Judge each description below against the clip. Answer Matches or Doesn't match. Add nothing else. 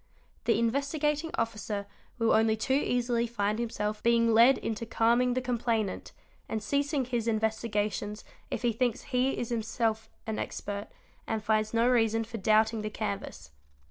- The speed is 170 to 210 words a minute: Doesn't match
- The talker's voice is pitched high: Matches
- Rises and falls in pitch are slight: Matches